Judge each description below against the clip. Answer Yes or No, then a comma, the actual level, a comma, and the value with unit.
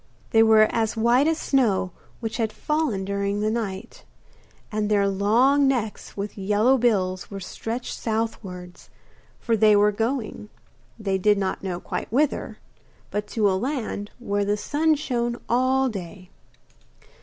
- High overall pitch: Yes, high, 215 Hz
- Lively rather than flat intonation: No, average, 3.3 semitones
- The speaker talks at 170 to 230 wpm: No, average, 145 wpm